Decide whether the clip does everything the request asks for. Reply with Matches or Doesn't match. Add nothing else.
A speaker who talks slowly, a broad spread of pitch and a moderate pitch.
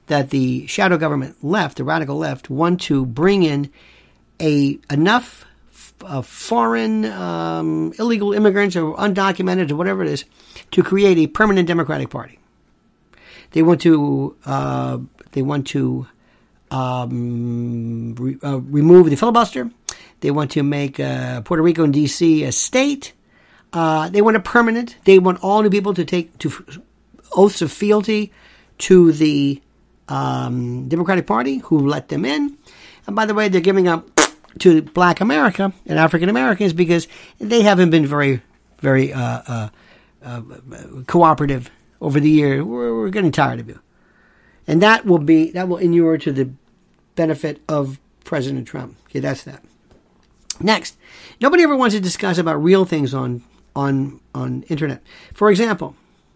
Doesn't match